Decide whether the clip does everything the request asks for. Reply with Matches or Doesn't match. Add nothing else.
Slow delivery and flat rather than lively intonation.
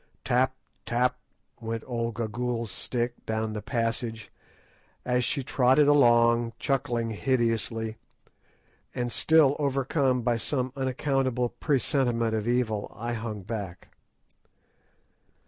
Matches